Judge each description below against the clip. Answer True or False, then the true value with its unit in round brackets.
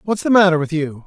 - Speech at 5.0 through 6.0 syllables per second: False (6.3 syllables/s)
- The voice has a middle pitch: True (170 Hz)